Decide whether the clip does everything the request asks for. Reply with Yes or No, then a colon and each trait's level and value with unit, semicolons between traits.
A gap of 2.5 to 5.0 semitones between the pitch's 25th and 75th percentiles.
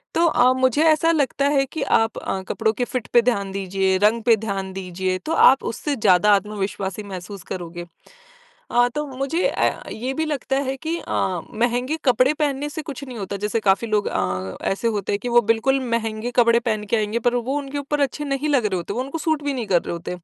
No: wide, 5.5 semitones